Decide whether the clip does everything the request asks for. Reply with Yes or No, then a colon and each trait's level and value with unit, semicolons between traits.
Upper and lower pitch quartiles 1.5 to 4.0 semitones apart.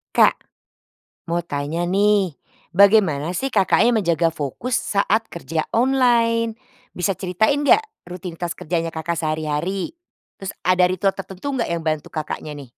No: average, 5.0 semitones